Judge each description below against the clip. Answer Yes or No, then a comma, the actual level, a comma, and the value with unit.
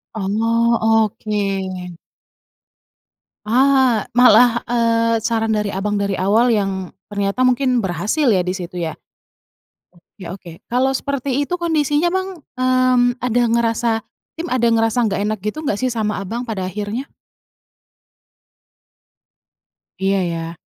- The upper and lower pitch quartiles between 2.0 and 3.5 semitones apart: No, average, 4.2 semitones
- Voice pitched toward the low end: No, high, 225 Hz